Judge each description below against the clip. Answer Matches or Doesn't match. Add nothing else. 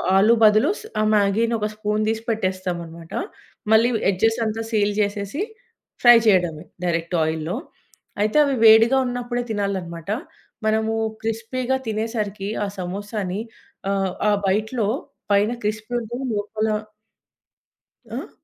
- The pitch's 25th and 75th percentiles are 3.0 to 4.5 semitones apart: Doesn't match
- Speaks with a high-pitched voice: Matches